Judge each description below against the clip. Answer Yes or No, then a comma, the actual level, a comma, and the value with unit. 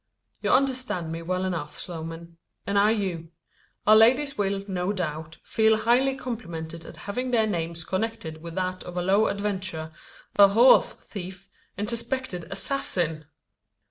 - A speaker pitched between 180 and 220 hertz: Yes, high, 190 Hz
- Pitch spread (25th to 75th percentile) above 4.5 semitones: Yes, average, 4.9 semitones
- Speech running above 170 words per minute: No, average, 145 wpm